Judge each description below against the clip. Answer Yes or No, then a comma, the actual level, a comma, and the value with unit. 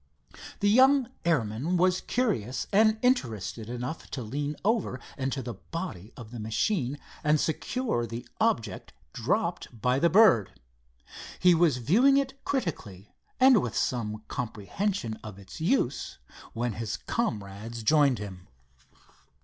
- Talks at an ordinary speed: No, slow, 130 wpm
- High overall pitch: No, low, 135 Hz